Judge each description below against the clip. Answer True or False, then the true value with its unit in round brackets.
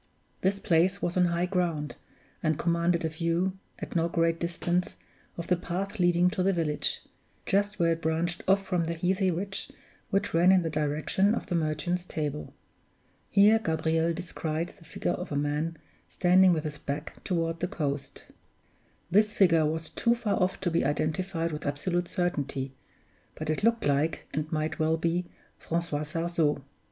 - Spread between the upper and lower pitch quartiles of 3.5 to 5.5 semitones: False (2.5 semitones)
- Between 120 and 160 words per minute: False (170 wpm)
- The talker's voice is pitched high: False (170 Hz)